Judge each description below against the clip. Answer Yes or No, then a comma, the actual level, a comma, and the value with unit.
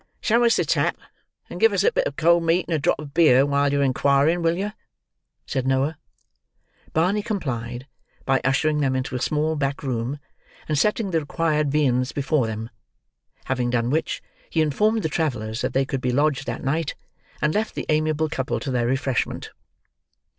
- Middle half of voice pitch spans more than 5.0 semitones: No, average, 3.8 semitones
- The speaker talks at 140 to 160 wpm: No, average, 185 wpm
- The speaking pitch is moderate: Yes, medium, 145 Hz